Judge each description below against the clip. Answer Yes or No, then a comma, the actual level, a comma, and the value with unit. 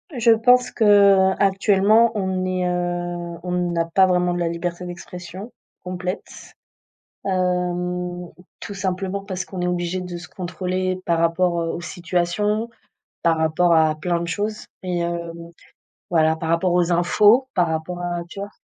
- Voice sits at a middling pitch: Yes, medium, 180 Hz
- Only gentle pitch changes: Yes, narrow, 1.7 semitones